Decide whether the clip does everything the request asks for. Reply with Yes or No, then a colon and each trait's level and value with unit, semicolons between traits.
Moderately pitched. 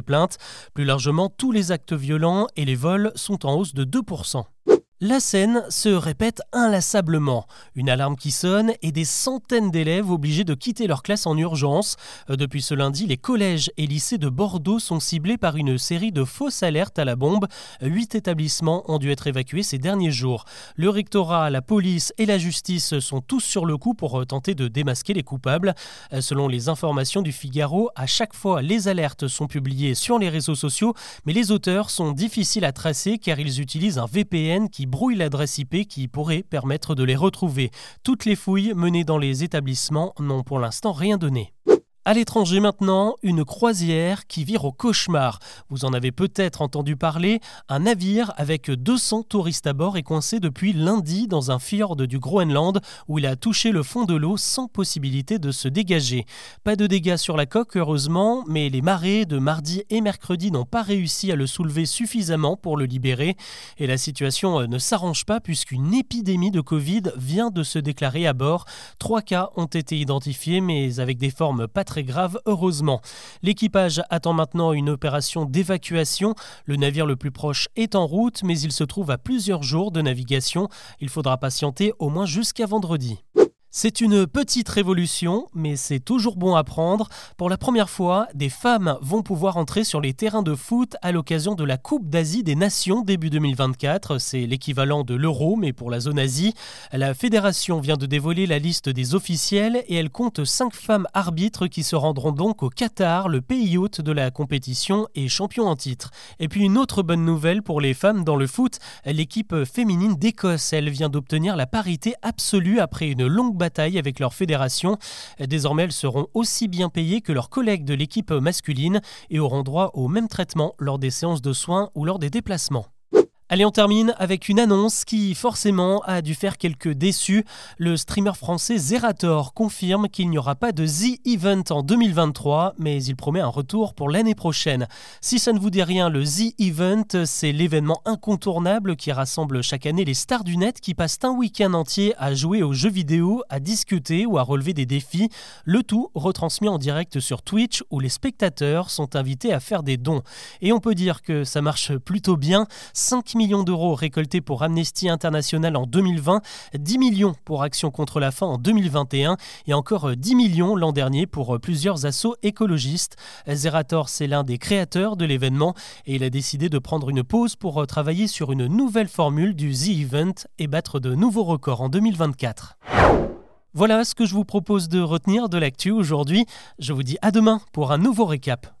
Yes: medium, 170 Hz